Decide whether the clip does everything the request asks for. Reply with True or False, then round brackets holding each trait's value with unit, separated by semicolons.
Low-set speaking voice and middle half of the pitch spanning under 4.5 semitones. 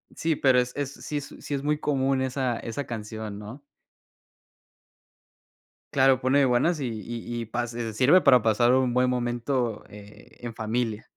True (125 Hz; 2.8 semitones)